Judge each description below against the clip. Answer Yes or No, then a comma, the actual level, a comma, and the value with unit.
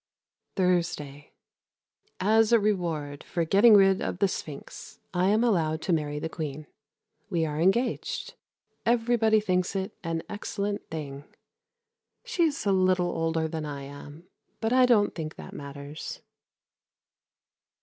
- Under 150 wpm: Yes, slow, 135 wpm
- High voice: No, medium, 180 Hz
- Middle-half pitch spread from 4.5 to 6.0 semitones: Yes, average, 5.2 semitones